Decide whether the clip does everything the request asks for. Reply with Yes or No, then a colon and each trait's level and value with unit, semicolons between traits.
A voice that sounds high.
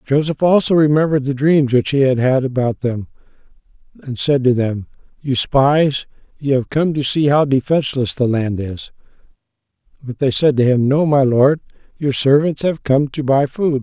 No: medium, 140 Hz